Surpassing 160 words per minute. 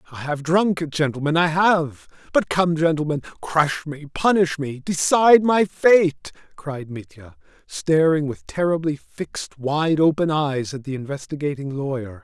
No: average, 145 wpm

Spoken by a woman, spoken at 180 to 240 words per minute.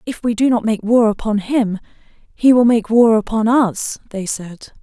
Yes: female; average, 200 wpm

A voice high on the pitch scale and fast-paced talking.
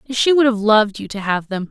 Yes: high, 220 Hz; fast, 280 wpm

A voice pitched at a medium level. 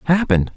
Yes: medium, 145 Hz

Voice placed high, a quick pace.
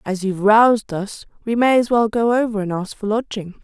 Yes: high, 215 Hz; fast, 230 wpm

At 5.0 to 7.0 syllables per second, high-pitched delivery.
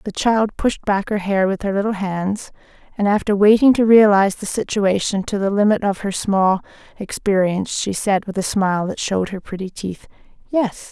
Yes: 5.1 syllables/s; high, 200 Hz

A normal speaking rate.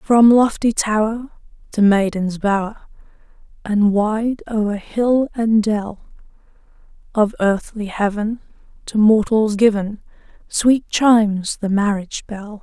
No: slow, 110 wpm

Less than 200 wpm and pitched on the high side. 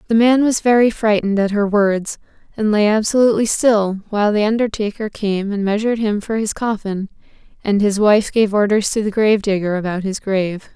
Yes: average, 185 wpm; high, 210 Hz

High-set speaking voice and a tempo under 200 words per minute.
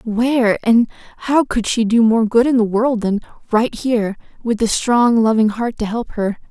No: high, 230 Hz; fast, 205 wpm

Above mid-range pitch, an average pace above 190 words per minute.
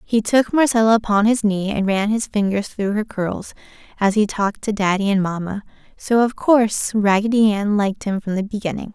Yes: high, 210 Hz; average, 200 wpm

